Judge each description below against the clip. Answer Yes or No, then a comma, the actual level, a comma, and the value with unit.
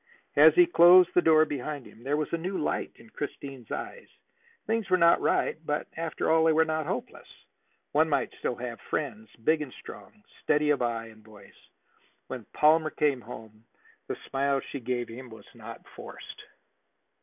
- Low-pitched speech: No, medium, 145 Hz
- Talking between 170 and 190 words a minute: Yes, average, 180 wpm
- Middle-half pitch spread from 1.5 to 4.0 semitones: No, average, 4.8 semitones